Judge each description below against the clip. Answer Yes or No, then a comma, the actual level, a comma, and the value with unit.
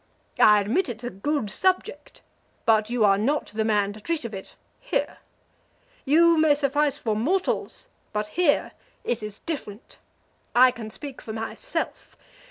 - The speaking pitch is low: No, high, 240 Hz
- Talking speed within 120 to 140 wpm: No, average, 155 wpm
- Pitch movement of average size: No, wide, 5.9 semitones